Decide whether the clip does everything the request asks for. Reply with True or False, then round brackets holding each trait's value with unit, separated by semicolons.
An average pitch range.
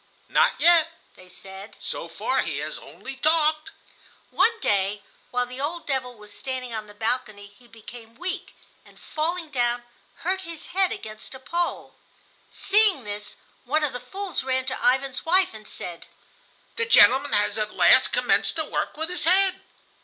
False (7.1 semitones)